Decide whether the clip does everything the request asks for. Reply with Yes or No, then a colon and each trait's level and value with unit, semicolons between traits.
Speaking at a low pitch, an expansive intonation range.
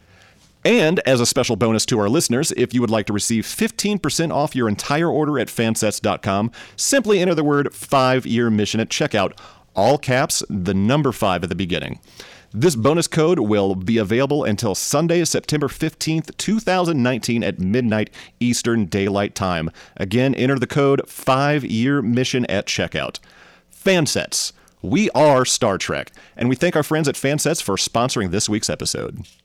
Yes: low, 125 Hz; wide, 5.7 semitones